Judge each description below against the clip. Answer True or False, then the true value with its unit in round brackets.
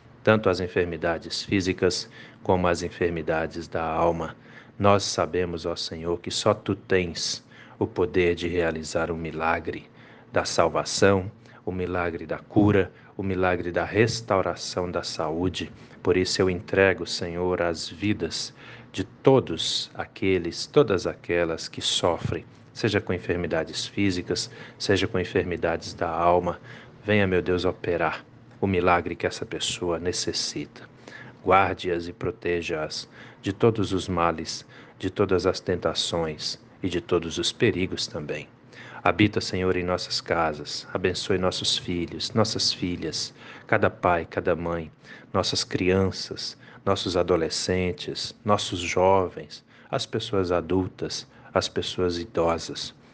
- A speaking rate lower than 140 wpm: True (125 wpm)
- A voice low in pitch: True (90 Hz)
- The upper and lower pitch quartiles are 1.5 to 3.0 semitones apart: False (3.5 semitones)